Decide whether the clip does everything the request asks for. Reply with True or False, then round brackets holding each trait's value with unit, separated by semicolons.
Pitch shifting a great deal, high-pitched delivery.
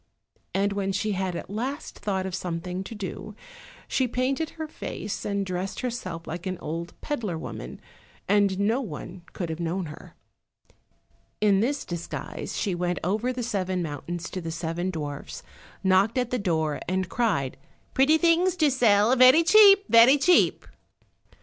True (5.9 semitones; 200 Hz)